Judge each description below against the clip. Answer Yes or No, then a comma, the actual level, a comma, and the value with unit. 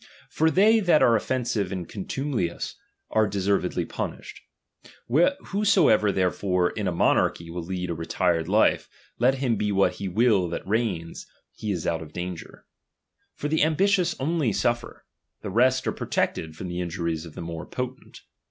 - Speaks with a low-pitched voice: Yes, low, 100 Hz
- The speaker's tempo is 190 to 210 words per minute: No, average, 175 wpm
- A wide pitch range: Yes, wide, 6.9 semitones